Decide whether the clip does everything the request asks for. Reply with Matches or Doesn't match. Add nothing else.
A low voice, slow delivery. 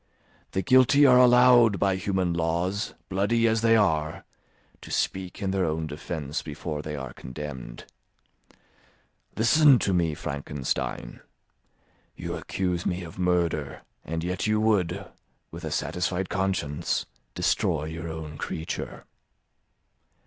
Matches